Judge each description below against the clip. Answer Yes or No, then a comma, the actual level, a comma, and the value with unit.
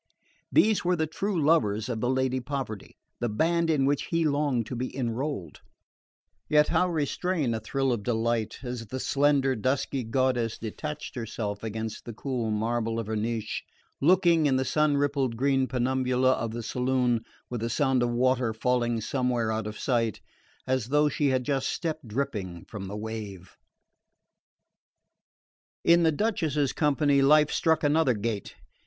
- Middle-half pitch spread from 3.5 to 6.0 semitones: Yes, average, 4.2 semitones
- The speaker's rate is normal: Yes, average, 160 wpm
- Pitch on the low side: Yes, low, 130 Hz